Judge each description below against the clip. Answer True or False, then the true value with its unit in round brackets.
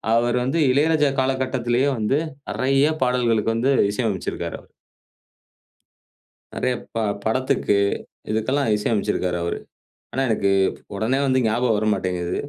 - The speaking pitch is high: False (120 Hz)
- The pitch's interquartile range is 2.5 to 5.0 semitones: True (3.5 semitones)